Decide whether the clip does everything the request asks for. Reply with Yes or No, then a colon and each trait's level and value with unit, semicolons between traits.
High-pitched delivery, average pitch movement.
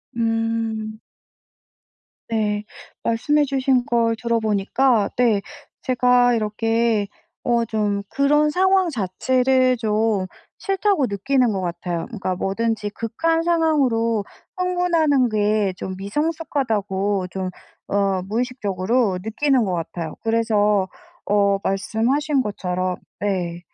Yes: high, 225 Hz; average, 4.4 semitones